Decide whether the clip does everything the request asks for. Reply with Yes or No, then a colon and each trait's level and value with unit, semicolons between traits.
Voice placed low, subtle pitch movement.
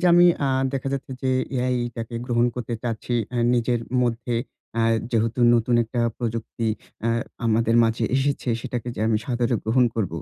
Yes: low, 120 Hz; narrow, 1.8 semitones